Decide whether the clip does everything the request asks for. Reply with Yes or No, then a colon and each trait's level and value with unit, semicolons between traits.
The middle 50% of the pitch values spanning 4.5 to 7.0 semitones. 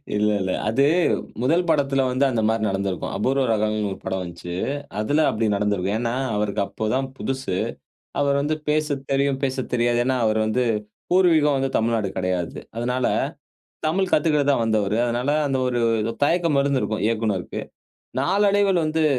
Yes: average, 5.0 semitones